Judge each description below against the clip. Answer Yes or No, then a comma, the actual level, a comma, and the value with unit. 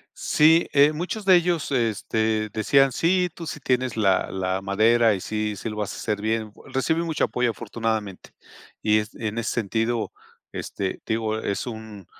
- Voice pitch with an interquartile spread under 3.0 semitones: No, average, 4.4 semitones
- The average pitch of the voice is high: No, low, 110 Hz